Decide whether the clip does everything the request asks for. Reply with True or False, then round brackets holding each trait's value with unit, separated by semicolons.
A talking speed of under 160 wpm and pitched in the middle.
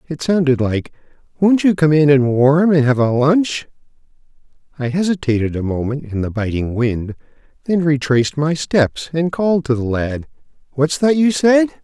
False (165 wpm; 145 Hz)